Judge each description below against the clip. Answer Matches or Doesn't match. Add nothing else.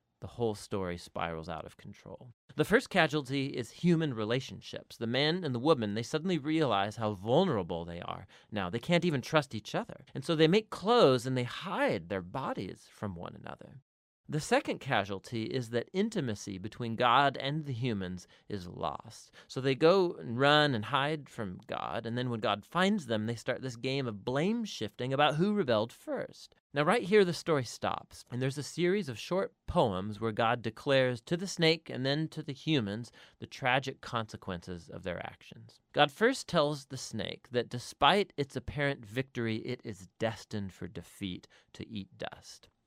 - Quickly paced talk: Doesn't match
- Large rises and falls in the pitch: Matches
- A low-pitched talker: Matches